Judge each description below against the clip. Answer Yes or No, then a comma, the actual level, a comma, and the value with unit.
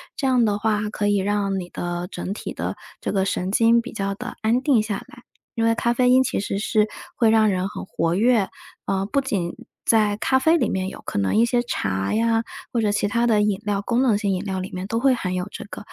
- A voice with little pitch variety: No, average, 3.3 semitones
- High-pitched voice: Yes, high, 210 Hz